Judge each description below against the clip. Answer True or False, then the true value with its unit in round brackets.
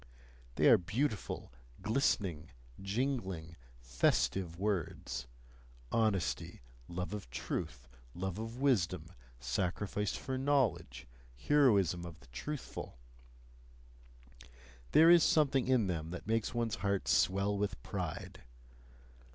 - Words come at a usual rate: False (100 wpm)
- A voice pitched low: True (100 Hz)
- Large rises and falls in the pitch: True (5.7 semitones)